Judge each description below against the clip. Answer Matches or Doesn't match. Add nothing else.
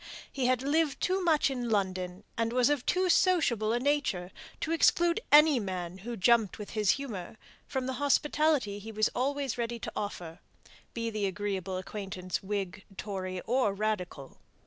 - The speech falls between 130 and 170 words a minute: Matches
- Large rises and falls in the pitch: Matches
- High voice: Matches